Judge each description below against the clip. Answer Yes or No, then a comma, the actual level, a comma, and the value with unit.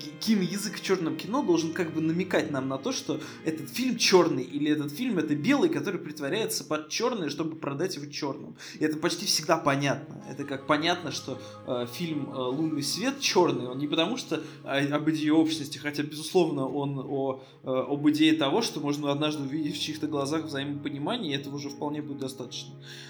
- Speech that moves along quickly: Yes, fast, 185 wpm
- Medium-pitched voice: Yes, medium, 150 Hz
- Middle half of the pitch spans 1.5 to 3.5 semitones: Yes, average, 2.8 semitones